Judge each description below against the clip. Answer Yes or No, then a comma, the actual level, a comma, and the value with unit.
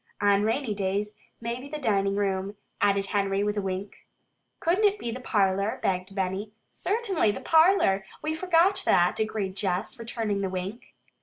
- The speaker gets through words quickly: No, average, 160 wpm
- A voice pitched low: No, high, 205 Hz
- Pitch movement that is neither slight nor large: Yes, average, 4.5 semitones